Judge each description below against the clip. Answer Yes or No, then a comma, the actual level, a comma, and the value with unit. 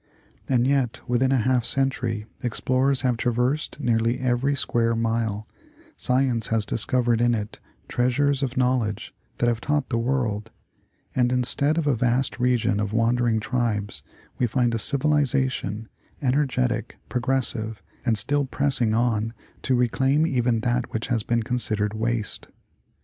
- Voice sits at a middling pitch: No, low, 120 Hz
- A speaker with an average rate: Yes, average, 150 wpm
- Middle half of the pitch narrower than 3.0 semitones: Yes, narrow, 2.5 semitones